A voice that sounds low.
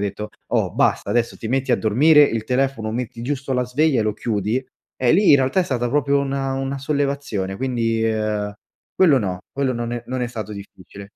Yes: low, 125 Hz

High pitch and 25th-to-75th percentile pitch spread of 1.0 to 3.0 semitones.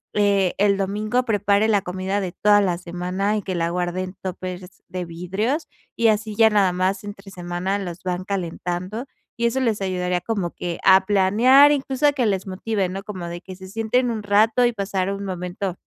Yes: high, 195 Hz; average, 2.7 semitones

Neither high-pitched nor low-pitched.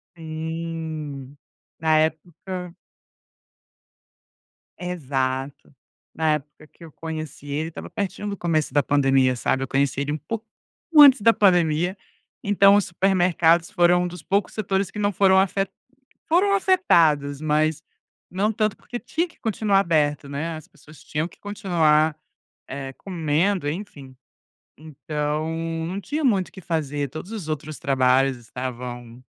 Yes: medium, 160 Hz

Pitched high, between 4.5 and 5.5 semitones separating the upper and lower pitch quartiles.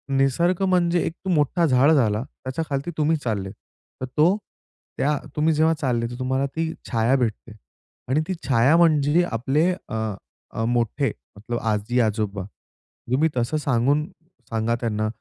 No: low, 130 Hz; average, 5.1 semitones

